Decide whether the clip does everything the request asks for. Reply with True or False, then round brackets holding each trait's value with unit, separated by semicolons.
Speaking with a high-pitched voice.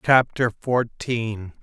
False (115 Hz)